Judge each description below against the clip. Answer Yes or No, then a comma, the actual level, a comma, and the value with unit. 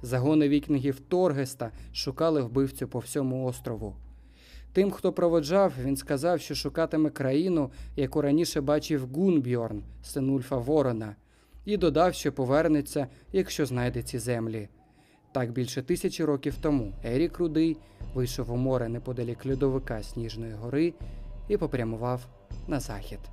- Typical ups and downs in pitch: Yes, average, 4.3 semitones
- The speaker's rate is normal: Yes, average, 125 wpm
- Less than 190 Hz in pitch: Yes, low, 135 Hz